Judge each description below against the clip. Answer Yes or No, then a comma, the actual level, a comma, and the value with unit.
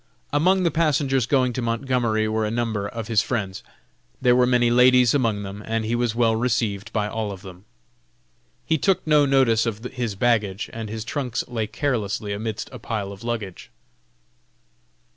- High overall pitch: No, low, 115 Hz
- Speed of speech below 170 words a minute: No, average, 175 wpm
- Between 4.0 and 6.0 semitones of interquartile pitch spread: No, average, 3.0 semitones